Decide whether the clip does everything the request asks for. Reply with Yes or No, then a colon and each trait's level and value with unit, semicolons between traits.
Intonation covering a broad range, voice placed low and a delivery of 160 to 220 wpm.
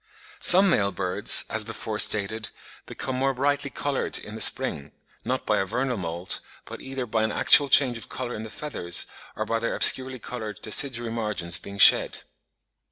No: average, 4.0 semitones; low, 115 Hz; average, 175 wpm